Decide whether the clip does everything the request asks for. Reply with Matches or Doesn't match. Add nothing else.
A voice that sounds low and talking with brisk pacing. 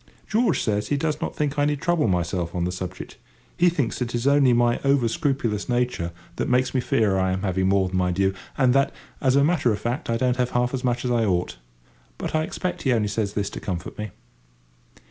Matches